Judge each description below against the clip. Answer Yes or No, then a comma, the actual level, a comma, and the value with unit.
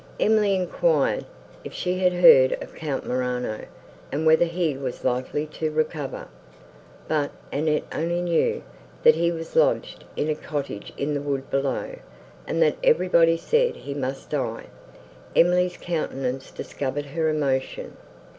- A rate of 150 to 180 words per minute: No, average, 140 wpm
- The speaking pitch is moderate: Yes, medium, 155 Hz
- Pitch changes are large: No, average, 4.3 semitones